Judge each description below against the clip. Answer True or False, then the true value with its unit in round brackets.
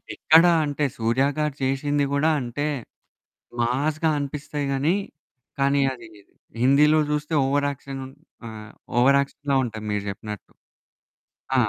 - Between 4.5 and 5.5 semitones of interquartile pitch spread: False (2.8 semitones)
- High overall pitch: False (140 Hz)